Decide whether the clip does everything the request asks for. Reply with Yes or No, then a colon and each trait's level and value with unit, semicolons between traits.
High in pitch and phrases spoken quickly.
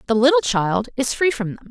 Yes: very high, 250 Hz; fast, 245 wpm